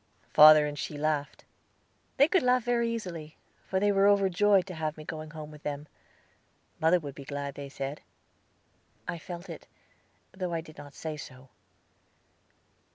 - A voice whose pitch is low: No, medium, 155 Hz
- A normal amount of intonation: Yes, average, 4.5 semitones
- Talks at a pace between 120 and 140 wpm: No, average, 160 wpm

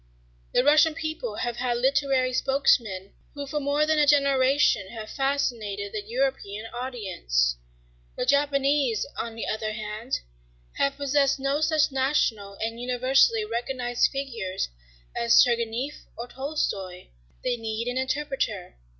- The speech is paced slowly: Yes, slow, 130 wpm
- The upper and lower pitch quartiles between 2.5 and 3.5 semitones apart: No, average, 4.0 semitones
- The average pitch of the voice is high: Yes, very high, 255 Hz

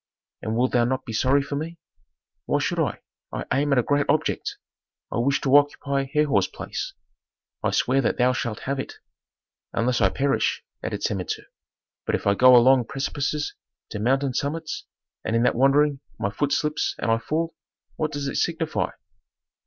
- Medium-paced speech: Yes, average, 175 wpm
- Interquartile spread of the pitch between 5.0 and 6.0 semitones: No, average, 3.1 semitones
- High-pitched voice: No, low, 135 Hz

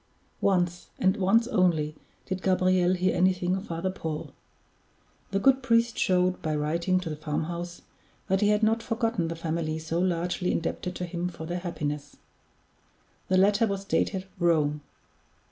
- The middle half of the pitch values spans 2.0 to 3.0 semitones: Yes, narrow, 2.4 semitones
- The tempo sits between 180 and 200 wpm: No, average, 155 wpm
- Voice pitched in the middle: Yes, medium, 180 Hz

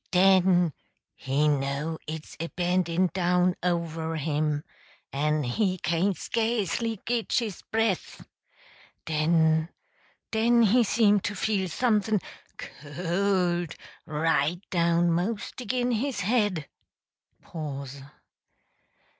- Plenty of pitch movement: No, average, 4.5 semitones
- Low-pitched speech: No, medium, 180 Hz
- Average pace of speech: No, slow, 110 wpm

